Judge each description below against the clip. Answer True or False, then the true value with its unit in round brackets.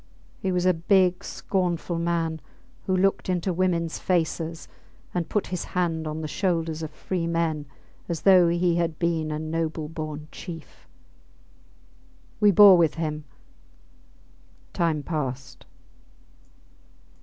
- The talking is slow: True (125 wpm)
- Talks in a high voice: False (170 Hz)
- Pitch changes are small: True (2.3 semitones)